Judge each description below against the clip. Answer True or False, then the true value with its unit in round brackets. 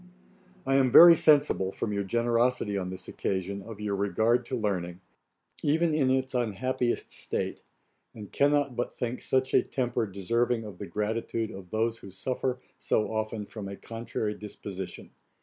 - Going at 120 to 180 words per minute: True (160 wpm)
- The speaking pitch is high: False (115 Hz)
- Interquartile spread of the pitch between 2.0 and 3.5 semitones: False (4.1 semitones)